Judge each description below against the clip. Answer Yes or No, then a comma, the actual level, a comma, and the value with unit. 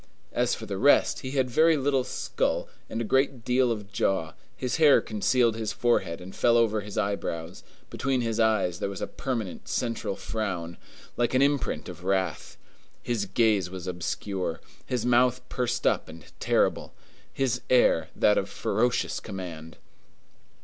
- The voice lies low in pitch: Yes, low, 115 Hz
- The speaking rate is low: No, average, 160 wpm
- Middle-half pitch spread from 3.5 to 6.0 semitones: Yes, average, 4.8 semitones